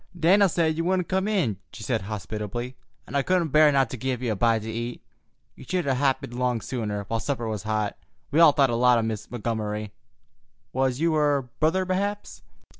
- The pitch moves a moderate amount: No, wide, 6.1 semitones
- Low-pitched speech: Yes, low, 125 Hz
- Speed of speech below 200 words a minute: No, fast, 205 wpm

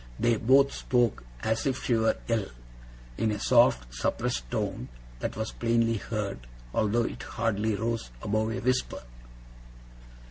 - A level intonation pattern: Yes, narrow, 2.1 semitones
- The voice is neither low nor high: No, low, 110 Hz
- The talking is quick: No, average, 140 wpm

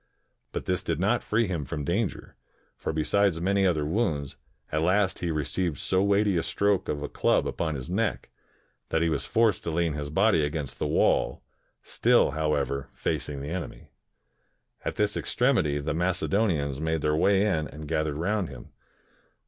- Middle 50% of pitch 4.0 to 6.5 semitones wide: Yes, average, 4.8 semitones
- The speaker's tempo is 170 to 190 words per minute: Yes, average, 175 wpm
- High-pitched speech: No, very low, 80 Hz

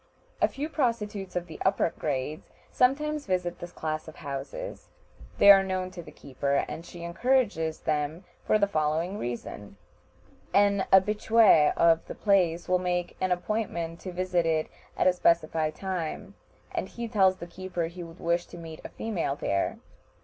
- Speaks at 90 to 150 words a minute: No, average, 165 wpm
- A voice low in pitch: No, medium, 175 Hz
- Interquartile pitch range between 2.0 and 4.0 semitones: Yes, average, 3.6 semitones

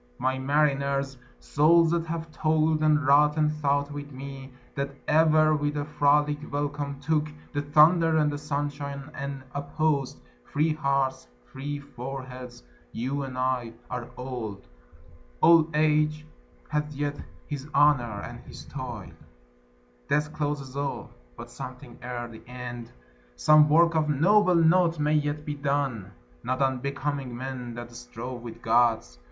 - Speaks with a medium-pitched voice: Yes, medium, 145 Hz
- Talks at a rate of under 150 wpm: Yes, average, 140 wpm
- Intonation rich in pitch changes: No, narrow, 2.6 semitones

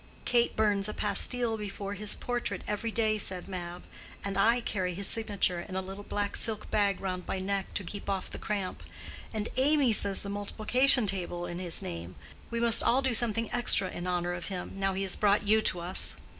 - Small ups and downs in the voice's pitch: No, average, 3.0 semitones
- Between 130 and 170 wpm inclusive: No, fast, 205 wpm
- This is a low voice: No, high, 200 Hz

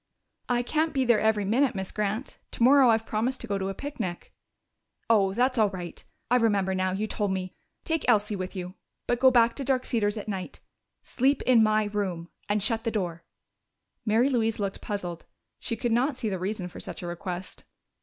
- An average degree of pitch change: Yes, average, 4.1 semitones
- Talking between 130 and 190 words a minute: No, average, 200 wpm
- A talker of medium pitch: No, high, 215 Hz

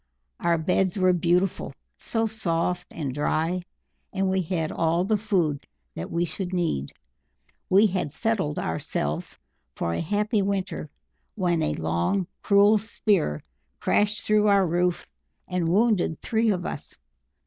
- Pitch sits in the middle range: Yes, medium, 180 Hz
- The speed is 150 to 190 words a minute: No, slow, 135 wpm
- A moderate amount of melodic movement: Yes, average, 3.7 semitones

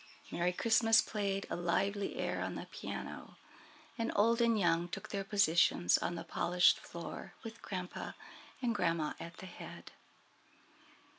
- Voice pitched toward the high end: Yes, high, 195 Hz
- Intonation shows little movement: No, average, 4.1 semitones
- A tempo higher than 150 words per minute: No, average, 145 wpm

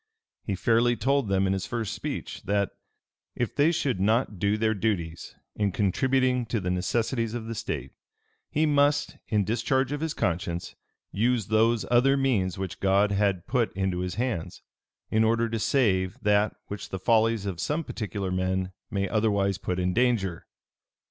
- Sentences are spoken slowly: No, average, 170 wpm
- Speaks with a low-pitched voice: Yes, low, 105 Hz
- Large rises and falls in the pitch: No, average, 4.0 semitones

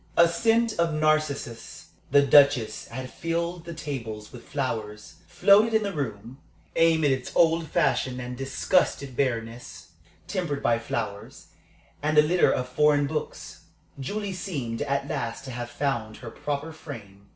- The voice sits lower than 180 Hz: Yes, medium, 140 Hz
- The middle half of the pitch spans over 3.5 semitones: Yes, wide, 5.4 semitones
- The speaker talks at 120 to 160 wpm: Yes, average, 145 wpm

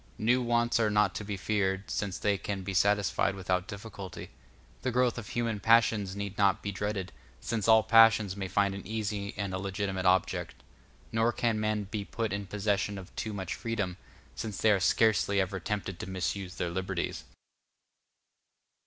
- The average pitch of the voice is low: Yes, low, 100 Hz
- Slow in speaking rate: No, average, 175 wpm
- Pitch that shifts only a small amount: Yes, narrow, 2.3 semitones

